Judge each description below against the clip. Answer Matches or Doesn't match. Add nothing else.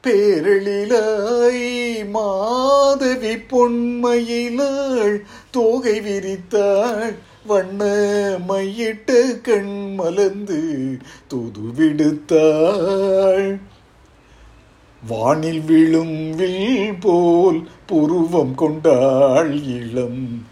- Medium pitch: Doesn't match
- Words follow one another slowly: Matches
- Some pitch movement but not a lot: Doesn't match